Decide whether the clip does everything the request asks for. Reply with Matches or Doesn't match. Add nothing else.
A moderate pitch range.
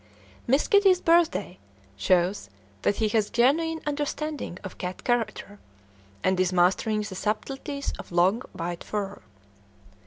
Doesn't match